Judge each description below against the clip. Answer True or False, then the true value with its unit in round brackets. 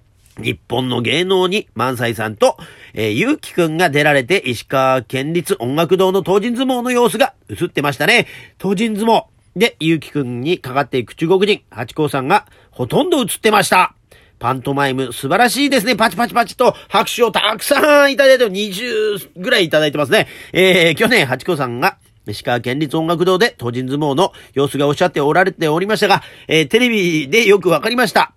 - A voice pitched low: False (170 Hz)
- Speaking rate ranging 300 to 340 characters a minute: False (380 characters per minute)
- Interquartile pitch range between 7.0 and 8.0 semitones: False (8.4 semitones)